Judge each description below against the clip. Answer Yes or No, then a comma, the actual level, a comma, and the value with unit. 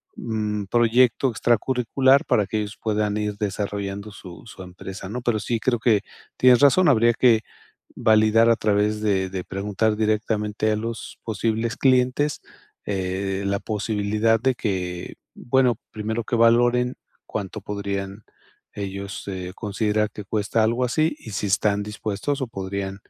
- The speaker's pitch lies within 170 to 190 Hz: No, low, 105 Hz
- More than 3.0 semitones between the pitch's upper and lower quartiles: No, average, 2.7 semitones